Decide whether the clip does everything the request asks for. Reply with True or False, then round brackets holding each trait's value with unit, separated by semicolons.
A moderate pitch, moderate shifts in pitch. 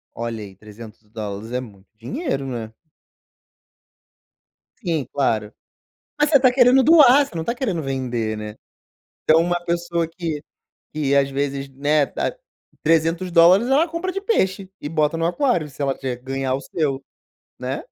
False (150 Hz; 6.4 semitones)